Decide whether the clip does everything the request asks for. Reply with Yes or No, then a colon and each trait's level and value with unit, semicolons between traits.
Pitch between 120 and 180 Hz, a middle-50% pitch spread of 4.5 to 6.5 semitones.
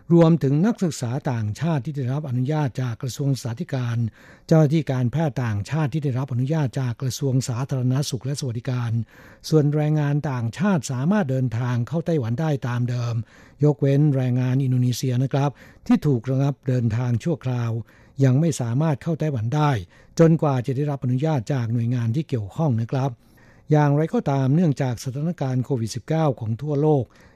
No: low, 135 Hz; average, 3.5 semitones